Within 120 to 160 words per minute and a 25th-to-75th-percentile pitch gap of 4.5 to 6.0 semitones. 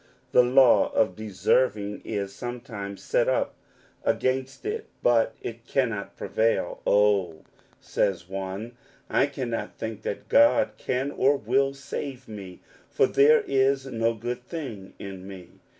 Yes: average, 140 wpm; average, 4.9 semitones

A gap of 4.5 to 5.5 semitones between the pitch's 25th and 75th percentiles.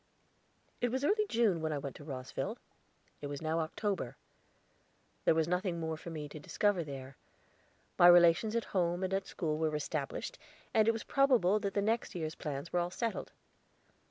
Yes: average, 5.1 semitones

